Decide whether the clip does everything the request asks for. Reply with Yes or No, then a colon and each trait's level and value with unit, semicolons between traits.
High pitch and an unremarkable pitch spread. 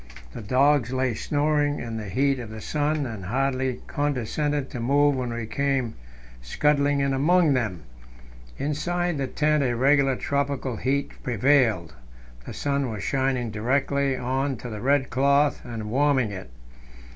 No: low, 135 Hz; average, 3.2 semitones